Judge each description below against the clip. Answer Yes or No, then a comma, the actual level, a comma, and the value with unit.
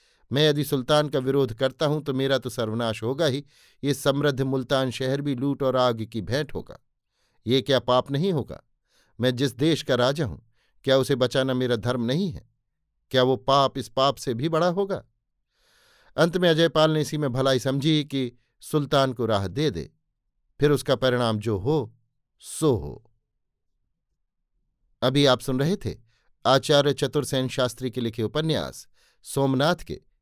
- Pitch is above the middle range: No, low, 135 Hz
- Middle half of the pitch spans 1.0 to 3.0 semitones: Yes, average, 2.7 semitones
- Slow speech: No, average, 170 wpm